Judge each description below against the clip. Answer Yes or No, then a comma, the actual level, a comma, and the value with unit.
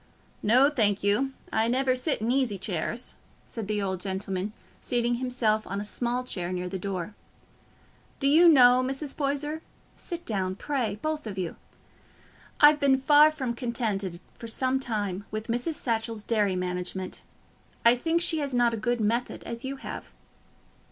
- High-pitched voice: Yes, high, 235 Hz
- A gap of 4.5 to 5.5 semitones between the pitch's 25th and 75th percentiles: Yes, average, 4.8 semitones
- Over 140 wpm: Yes, average, 160 wpm